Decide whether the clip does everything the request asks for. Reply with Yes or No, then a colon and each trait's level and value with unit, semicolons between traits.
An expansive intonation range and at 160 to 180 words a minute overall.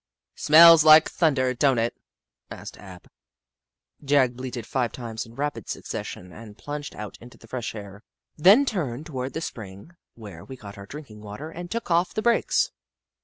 Yes: wide, 6.3 semitones; average, 175 wpm